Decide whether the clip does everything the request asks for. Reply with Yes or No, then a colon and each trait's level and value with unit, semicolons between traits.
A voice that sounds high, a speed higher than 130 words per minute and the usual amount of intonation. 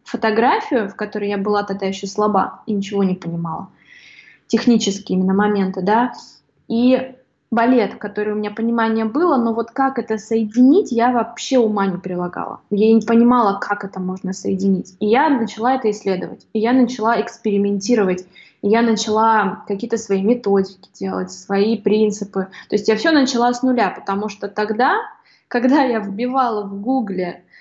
Yes: high, 215 Hz; fast, 160 wpm; average, 3.1 semitones